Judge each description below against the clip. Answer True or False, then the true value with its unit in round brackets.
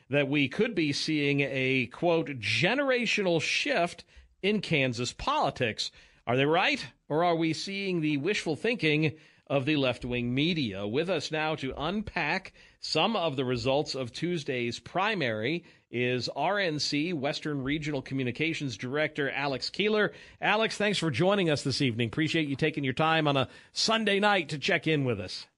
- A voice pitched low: False (155 Hz)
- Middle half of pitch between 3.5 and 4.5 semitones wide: True (4.1 semitones)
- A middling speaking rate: True (160 wpm)